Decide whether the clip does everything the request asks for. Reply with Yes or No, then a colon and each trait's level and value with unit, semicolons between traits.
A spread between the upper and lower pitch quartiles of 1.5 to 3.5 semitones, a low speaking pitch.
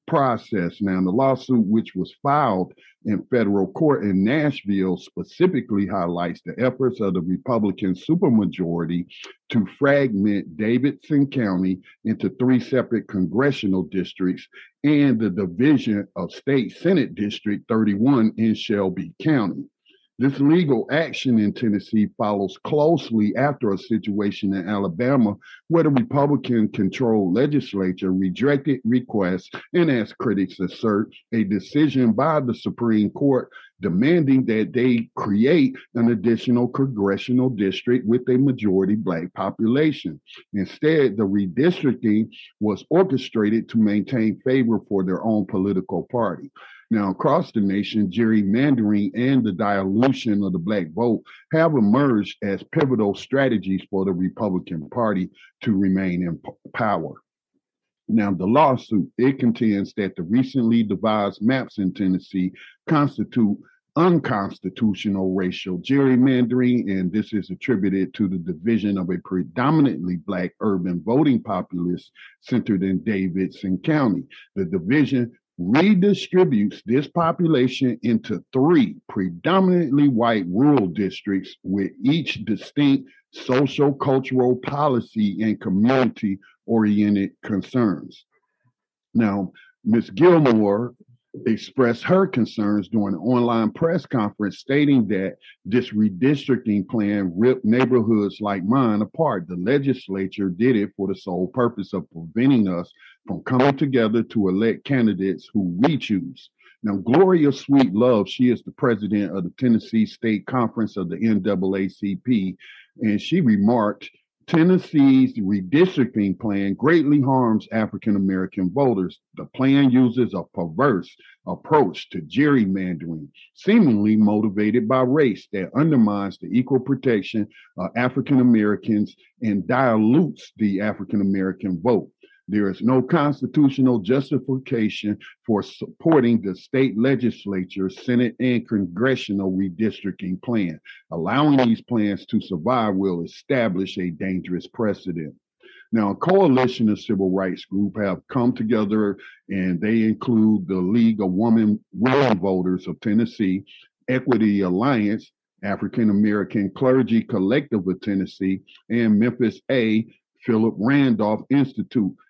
No: average, 4.8 semitones; low, 110 Hz